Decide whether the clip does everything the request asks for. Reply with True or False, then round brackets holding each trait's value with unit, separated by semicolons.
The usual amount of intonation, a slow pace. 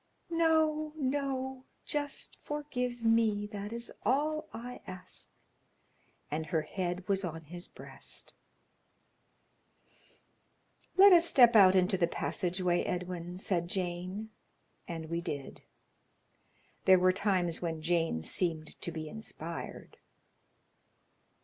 False (6.3 semitones; 110 wpm)